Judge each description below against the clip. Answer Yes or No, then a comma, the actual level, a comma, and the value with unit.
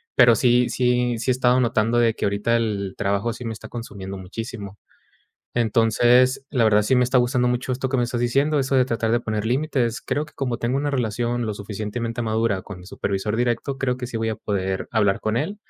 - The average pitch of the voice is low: Yes, low, 120 Hz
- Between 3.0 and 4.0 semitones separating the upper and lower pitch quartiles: No, narrow, 2.5 semitones